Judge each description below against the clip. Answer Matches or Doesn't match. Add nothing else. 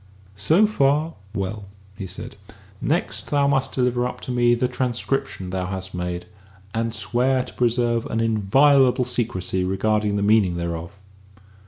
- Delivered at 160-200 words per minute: Doesn't match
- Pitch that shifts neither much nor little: Matches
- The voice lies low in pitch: Matches